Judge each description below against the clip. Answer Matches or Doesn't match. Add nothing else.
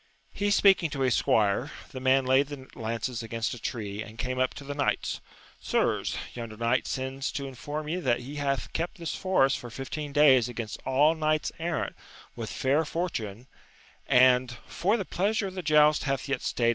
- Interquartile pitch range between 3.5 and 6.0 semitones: Matches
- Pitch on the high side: Doesn't match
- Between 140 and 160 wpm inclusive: Doesn't match